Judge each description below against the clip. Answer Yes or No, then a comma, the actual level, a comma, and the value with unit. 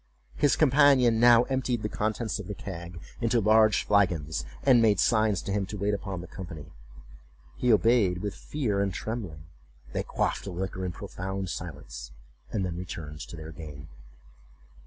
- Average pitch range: Yes, average, 4.5 semitones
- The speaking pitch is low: Yes, low, 100 Hz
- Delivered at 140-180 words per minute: Yes, average, 165 wpm